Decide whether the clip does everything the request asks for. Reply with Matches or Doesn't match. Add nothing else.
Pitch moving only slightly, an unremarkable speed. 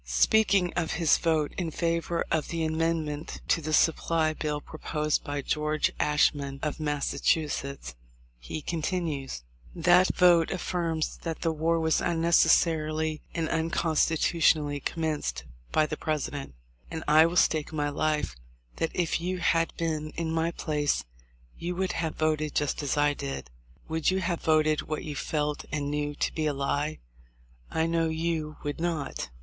Matches